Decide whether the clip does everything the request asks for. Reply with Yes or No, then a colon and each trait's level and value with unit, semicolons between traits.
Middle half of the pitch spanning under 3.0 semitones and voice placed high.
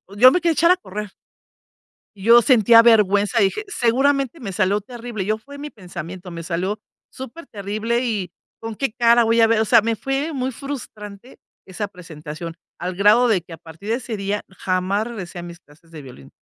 No: average, 4.4 semitones; high, 215 Hz